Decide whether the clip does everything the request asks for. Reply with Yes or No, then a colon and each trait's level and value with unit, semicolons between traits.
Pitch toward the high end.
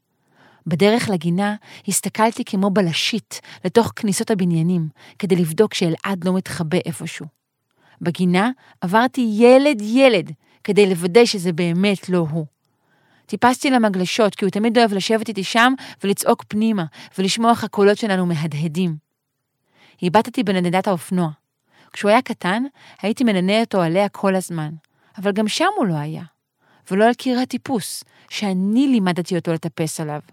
Yes: high, 195 Hz